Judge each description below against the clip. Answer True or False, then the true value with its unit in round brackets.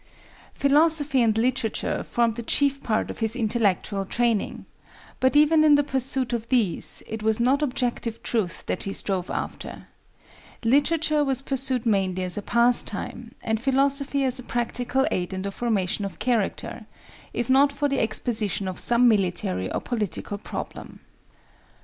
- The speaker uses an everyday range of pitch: True (4.1 semitones)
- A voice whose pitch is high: True (240 Hz)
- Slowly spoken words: False (150 wpm)